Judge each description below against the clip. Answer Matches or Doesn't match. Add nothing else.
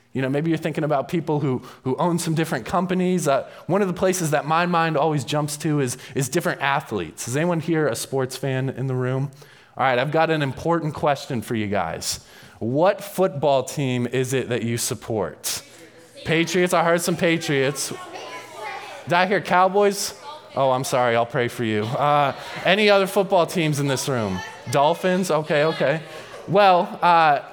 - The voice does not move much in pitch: Doesn't match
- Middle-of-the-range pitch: Matches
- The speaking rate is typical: Matches